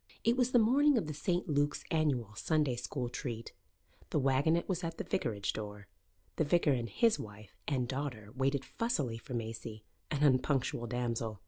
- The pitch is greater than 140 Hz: No, low, 135 Hz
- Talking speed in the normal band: Yes, average, 175 wpm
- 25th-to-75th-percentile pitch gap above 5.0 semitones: Yes, wide, 5.6 semitones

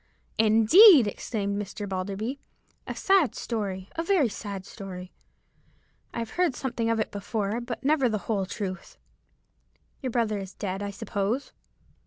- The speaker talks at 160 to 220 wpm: No, average, 140 wpm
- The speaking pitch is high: Yes, high, 215 Hz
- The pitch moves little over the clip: No, average, 3.8 semitones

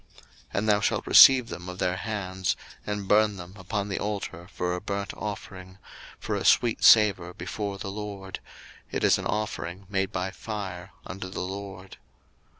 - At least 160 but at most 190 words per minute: Yes, average, 170 wpm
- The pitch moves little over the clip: Yes, narrow, 2.0 semitones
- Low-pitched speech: Yes, very low, 95 Hz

